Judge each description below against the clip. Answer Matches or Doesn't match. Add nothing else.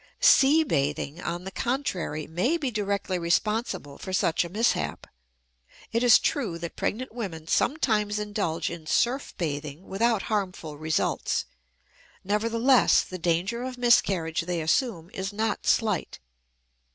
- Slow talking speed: Matches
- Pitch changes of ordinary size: Doesn't match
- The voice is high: Matches